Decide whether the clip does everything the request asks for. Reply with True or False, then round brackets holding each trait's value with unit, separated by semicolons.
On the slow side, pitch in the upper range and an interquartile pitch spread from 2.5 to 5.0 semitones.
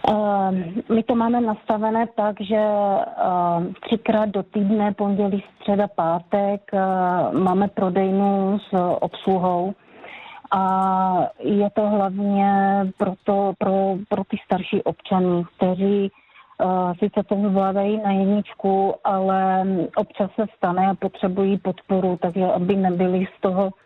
False (110 wpm; 195 Hz; 1.6 semitones)